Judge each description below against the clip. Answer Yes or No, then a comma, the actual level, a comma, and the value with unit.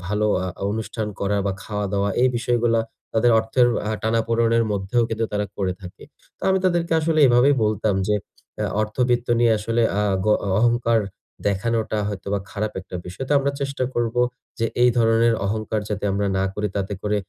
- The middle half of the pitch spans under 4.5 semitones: Yes, narrow, 2.5 semitones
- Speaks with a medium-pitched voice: No, low, 110 Hz